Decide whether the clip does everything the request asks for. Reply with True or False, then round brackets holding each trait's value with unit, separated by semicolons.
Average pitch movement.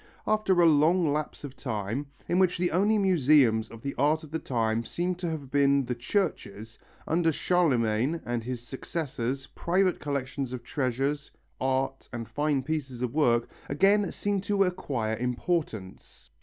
False (5.8 semitones)